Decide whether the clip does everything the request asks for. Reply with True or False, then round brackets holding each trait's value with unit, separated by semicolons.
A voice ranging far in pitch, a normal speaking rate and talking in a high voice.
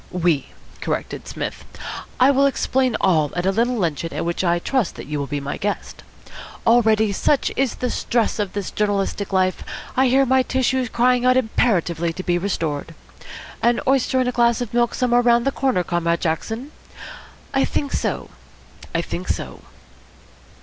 True (6.3 semitones; 170 wpm; 220 Hz)